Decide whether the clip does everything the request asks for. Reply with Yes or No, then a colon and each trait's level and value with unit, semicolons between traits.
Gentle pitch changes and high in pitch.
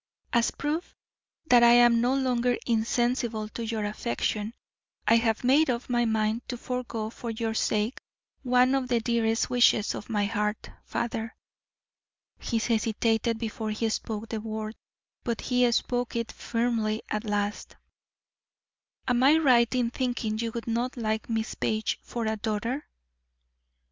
Yes: narrow, 1.9 semitones; high, 230 Hz